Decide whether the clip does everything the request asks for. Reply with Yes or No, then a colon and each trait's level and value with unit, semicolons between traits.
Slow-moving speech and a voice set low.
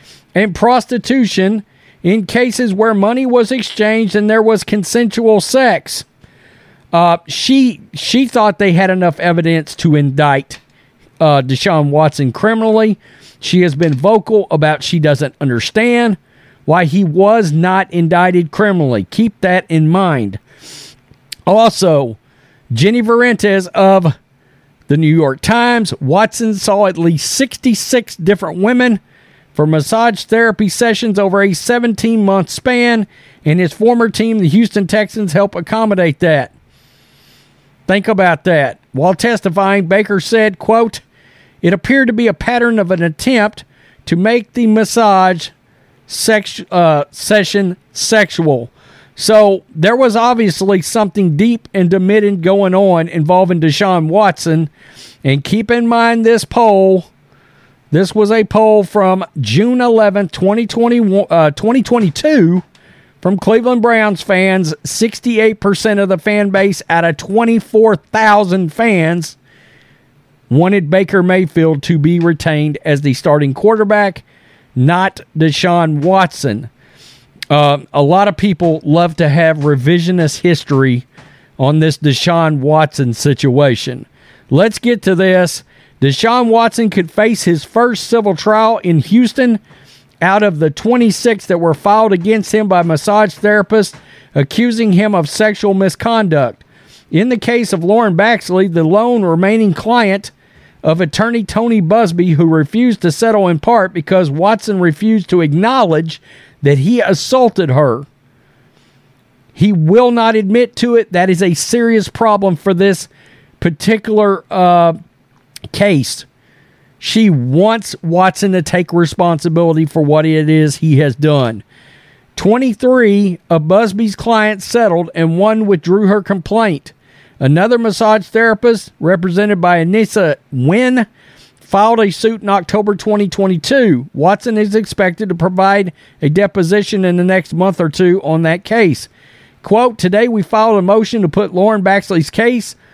No: slow, 130 wpm; high, 190 Hz